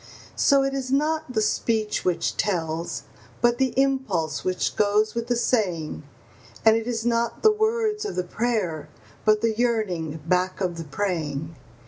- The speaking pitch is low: No, high, 220 Hz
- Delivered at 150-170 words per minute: Yes, average, 160 wpm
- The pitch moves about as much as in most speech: No, wide, 5.9 semitones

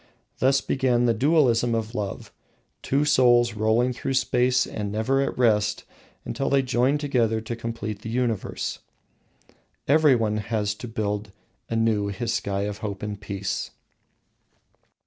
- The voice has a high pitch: No, low, 115 Hz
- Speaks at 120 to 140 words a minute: Yes, slow, 135 wpm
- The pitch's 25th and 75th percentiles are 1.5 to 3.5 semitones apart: Yes, average, 3.1 semitones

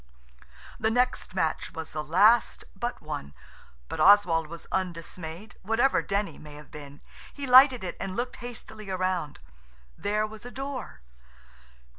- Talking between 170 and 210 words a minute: No, average, 140 wpm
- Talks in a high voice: Yes, high, 195 Hz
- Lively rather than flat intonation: Yes, wide, 6.5 semitones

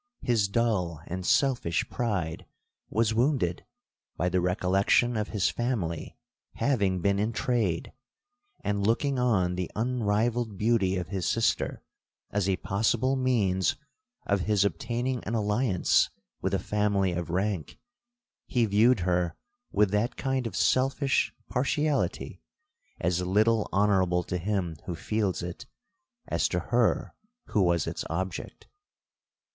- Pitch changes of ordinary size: Yes, average, 4.5 semitones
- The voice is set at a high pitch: No, low, 105 Hz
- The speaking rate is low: Yes, slow, 130 wpm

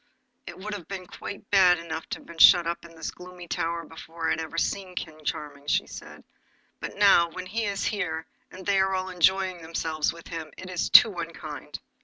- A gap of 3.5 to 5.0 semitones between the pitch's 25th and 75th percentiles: No, narrow, 2.6 semitones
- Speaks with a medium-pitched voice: Yes, medium, 175 Hz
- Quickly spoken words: Yes, fast, 210 wpm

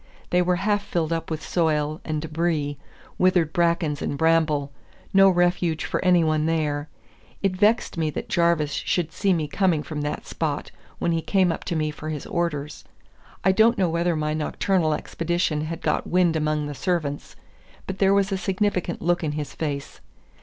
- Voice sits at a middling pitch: Yes, medium, 165 Hz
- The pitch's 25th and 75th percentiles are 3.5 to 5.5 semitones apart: No, average, 3.0 semitones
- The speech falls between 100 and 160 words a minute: No, average, 180 wpm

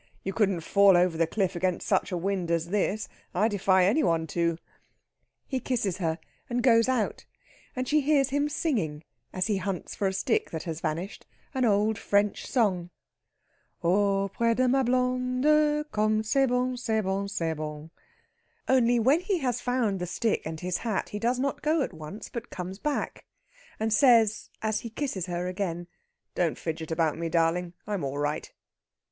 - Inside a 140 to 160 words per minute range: No, average, 180 wpm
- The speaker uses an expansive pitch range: Yes, wide, 6.1 semitones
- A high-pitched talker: Yes, high, 205 Hz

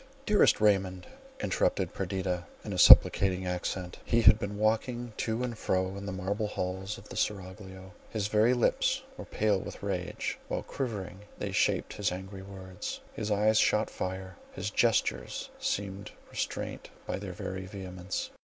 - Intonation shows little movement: Yes, narrow, 2.2 semitones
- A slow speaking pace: No, average, 150 wpm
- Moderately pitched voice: No, very low, 95 Hz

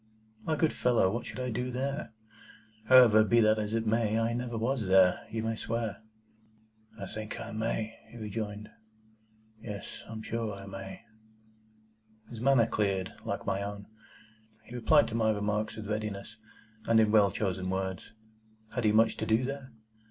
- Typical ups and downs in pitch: No, narrow, 2.2 semitones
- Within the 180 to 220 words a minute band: No, average, 170 wpm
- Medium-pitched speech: No, low, 110 Hz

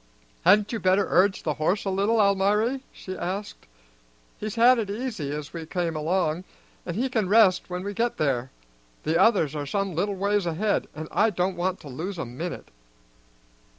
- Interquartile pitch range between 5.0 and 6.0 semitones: No, average, 4.0 semitones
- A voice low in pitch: No, high, 190 Hz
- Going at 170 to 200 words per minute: Yes, average, 185 wpm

